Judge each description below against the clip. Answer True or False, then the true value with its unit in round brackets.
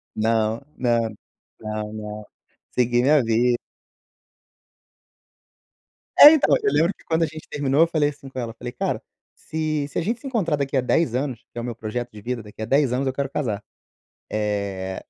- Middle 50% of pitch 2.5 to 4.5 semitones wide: False (5.1 semitones)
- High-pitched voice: False (125 Hz)